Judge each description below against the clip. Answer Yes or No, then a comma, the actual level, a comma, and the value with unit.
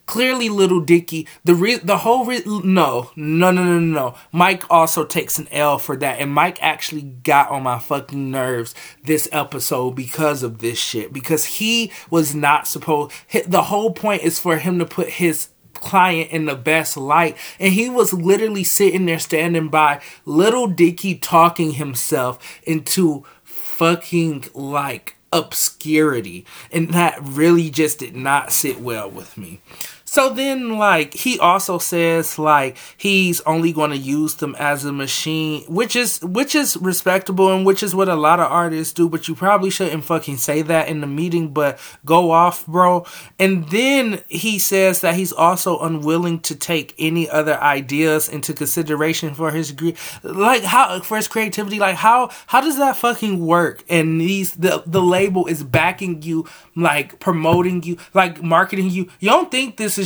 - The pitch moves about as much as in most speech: Yes, average, 3.7 semitones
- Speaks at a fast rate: No, average, 170 wpm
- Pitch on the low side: No, medium, 170 Hz